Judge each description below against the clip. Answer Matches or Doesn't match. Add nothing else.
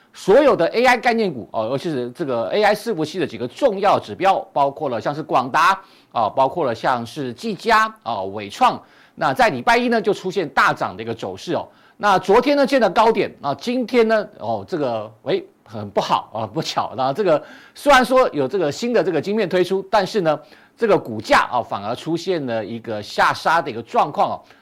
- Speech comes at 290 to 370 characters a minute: Matches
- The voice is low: Doesn't match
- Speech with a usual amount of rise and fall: Doesn't match